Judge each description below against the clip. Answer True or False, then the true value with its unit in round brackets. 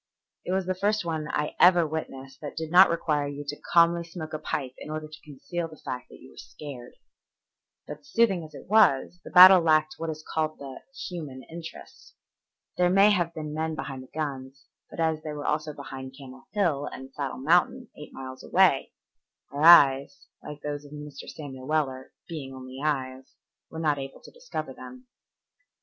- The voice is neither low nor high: True (155 Hz)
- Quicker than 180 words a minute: True (190 wpm)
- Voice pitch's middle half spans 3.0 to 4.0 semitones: True (3.4 semitones)